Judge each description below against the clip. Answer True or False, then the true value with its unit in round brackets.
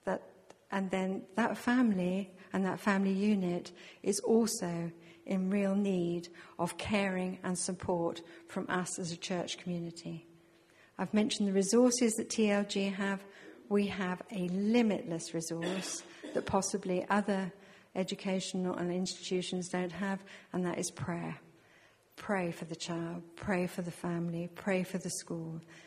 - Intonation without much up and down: True (2.3 semitones)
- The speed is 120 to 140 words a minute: True (135 wpm)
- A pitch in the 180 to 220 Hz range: True (185 Hz)